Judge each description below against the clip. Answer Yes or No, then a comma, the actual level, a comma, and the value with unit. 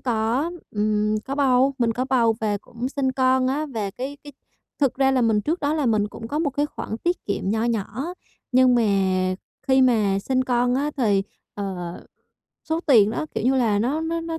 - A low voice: No, very high, 250 Hz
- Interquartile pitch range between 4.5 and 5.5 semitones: No, average, 4.0 semitones